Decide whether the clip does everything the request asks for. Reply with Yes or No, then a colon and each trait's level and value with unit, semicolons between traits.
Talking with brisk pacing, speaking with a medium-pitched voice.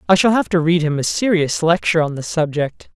Yes: fast, 240 wpm; medium, 165 Hz